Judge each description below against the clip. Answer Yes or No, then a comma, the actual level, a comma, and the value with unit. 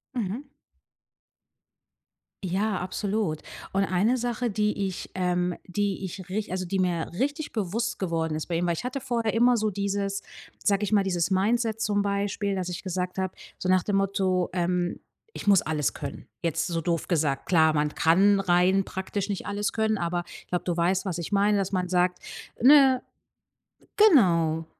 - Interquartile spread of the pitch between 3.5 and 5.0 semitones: No, average, 2.9 semitones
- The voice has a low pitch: No, high, 190 Hz